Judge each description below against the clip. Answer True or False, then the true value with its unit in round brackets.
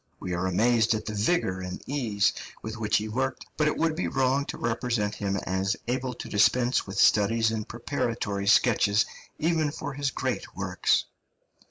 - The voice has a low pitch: True (115 Hz)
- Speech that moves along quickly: False (175 wpm)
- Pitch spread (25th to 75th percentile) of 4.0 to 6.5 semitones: True (4.3 semitones)